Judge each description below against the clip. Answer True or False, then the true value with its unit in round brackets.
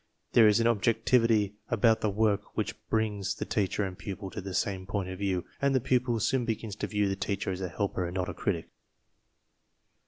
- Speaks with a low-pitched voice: True (105 Hz)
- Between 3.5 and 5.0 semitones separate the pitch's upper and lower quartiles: False (2.7 semitones)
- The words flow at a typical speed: False (215 wpm)